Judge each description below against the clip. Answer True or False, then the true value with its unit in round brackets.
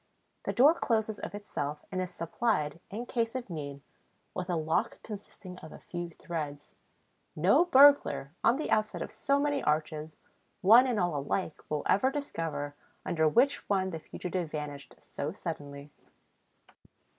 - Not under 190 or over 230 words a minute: False (155 wpm)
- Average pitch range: False (7.0 semitones)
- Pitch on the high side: False (180 Hz)